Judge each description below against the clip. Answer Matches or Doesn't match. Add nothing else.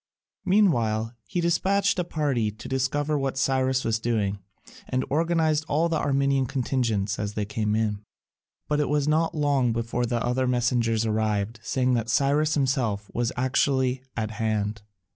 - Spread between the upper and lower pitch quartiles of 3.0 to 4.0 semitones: Doesn't match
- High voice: Doesn't match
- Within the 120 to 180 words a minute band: Matches